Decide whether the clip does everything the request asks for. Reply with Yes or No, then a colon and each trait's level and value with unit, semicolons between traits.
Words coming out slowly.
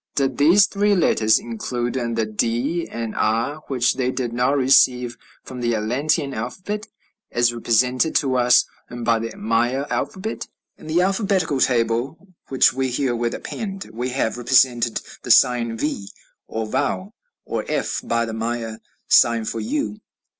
No: average, 145 wpm